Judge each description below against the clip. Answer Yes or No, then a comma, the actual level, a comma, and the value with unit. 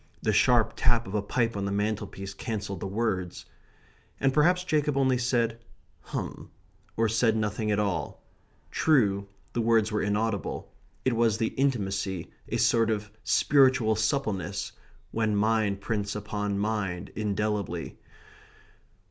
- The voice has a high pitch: No, low, 110 Hz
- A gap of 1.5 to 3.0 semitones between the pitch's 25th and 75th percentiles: Yes, narrow, 2.5 semitones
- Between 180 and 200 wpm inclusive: No, slow, 135 wpm